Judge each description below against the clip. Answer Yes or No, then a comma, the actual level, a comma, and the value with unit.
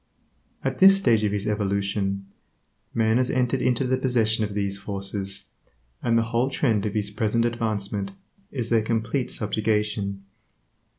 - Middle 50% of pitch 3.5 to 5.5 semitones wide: No, average, 2.8 semitones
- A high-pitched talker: No, low, 110 Hz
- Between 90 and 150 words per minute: Yes, average, 145 wpm